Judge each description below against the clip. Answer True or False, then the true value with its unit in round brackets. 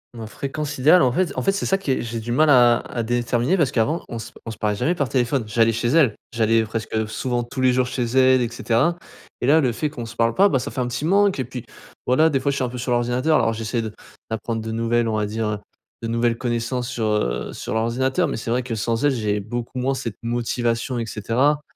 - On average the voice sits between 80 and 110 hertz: False (120 Hz)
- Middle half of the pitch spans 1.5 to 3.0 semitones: True (2.6 semitones)